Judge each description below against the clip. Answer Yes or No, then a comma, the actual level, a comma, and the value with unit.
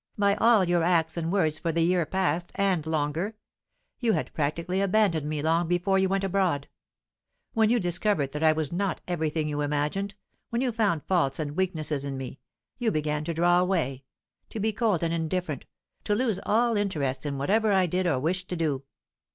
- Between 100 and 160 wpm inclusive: No, average, 190 wpm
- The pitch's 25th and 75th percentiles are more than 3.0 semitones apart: Yes, average, 4.3 semitones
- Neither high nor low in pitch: Yes, medium, 175 Hz